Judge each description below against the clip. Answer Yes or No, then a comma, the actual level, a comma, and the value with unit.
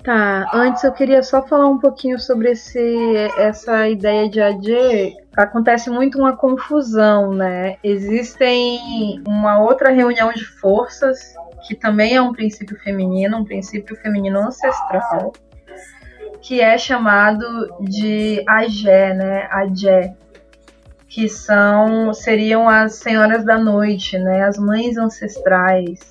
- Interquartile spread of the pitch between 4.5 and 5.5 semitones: No, average, 2.9 semitones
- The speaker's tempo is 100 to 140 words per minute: Yes, slow, 120 wpm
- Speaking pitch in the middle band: No, high, 220 Hz